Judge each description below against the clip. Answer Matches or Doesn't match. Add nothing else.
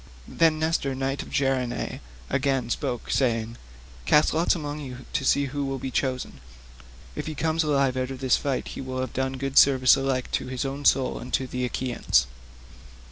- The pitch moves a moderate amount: Doesn't match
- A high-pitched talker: Doesn't match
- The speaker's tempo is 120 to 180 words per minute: Doesn't match